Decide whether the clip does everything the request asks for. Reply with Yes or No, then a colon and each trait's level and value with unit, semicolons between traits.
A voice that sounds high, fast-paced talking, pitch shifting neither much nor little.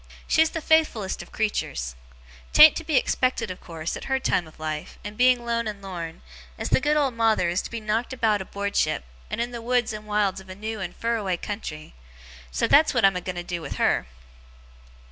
Yes: high, 210 Hz; fast, 220 wpm; average, 4.9 semitones